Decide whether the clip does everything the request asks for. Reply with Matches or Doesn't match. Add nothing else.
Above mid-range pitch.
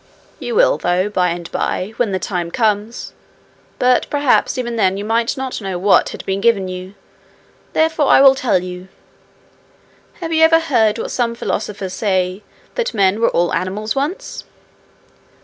Matches